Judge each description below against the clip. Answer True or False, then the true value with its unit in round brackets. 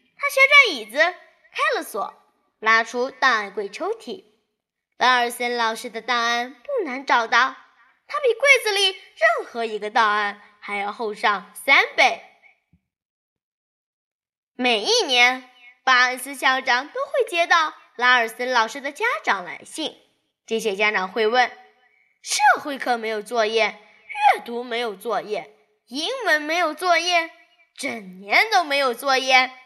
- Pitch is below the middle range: False (255 Hz)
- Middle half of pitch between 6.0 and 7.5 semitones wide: True (6.3 semitones)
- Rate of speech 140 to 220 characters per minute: True (200 characters per minute)